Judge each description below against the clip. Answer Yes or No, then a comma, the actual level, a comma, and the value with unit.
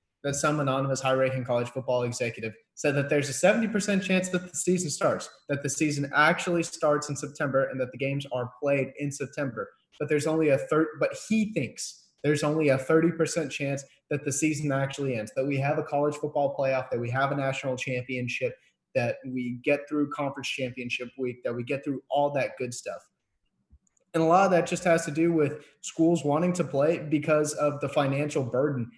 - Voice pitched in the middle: Yes, medium, 145 Hz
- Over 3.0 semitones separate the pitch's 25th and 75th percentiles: No, average, 2.7 semitones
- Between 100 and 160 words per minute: No, average, 200 wpm